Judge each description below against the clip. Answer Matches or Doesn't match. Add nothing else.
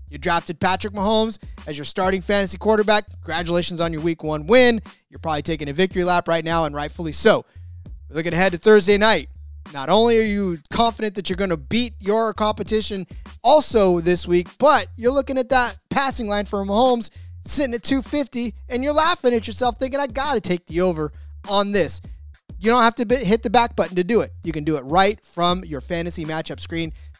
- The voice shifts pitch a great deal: Matches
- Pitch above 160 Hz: Matches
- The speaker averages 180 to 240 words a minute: Matches